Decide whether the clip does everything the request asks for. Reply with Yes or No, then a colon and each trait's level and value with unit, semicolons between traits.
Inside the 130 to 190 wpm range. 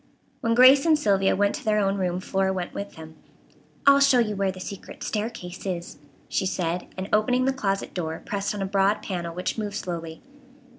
No: average, 200 wpm